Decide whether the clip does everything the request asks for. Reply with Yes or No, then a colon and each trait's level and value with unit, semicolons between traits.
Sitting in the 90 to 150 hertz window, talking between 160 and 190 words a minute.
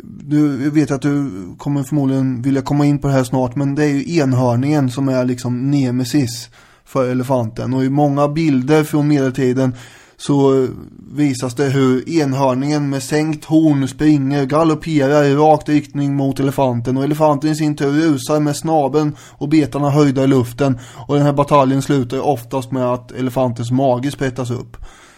Yes: medium, 140 Hz; average, 170 wpm